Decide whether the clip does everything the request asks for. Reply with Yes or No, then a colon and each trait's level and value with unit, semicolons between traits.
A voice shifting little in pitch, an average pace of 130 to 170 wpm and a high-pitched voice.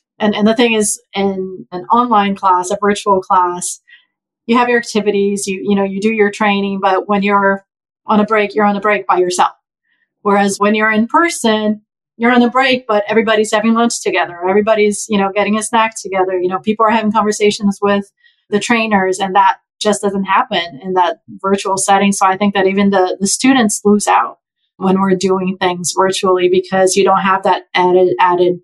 No: narrow, 2.1 semitones; average, 200 wpm; high, 200 Hz